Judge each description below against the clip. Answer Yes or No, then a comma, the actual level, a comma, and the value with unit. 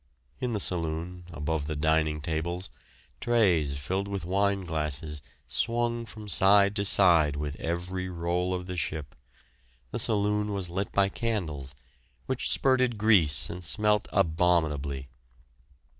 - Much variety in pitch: No, average, 4.4 semitones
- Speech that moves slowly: Yes, slow, 130 wpm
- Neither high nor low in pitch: No, very low, 90 Hz